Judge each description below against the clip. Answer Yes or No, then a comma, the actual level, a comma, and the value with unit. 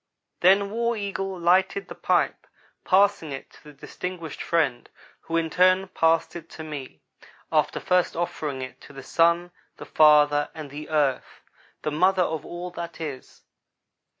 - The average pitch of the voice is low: No, medium, 165 Hz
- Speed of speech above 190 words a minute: No, average, 155 wpm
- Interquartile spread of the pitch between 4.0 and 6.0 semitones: No, average, 3.6 semitones